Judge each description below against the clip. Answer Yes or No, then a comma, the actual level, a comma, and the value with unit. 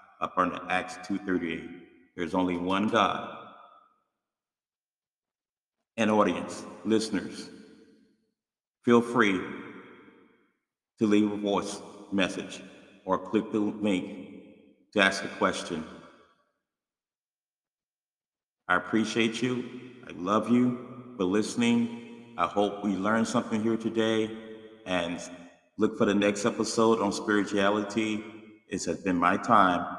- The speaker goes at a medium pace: No, slow, 110 wpm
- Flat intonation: Yes, narrow, 2.3 semitones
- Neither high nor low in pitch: No, low, 110 Hz